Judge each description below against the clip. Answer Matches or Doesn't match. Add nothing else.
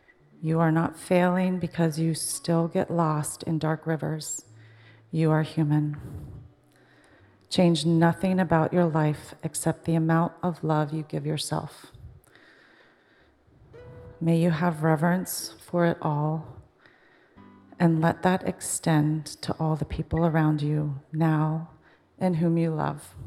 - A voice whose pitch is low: Doesn't match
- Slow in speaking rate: Matches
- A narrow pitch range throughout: Matches